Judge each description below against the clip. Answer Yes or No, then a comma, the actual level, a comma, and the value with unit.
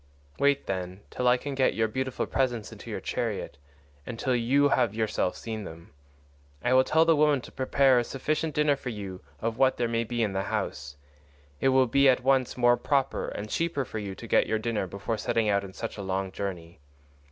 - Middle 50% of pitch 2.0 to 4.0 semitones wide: No, average, 4.9 semitones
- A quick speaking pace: Yes, fast, 215 wpm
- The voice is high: No, low, 120 Hz